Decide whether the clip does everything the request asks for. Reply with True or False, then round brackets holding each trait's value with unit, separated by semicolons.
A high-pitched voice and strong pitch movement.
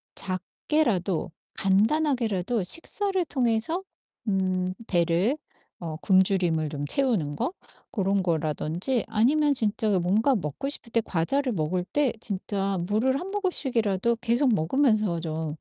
True (210 Hz; 6.6 semitones)